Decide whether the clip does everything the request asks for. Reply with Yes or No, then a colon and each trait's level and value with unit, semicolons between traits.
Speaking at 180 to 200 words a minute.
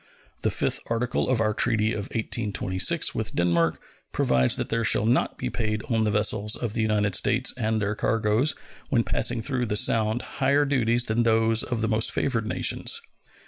Yes: average, 185 wpm